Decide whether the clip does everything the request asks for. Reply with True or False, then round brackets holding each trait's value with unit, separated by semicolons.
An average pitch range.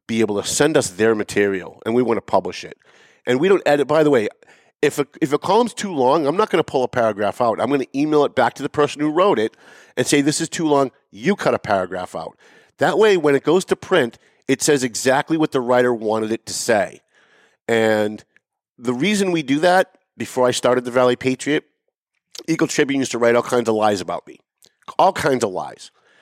True (4.7 semitones)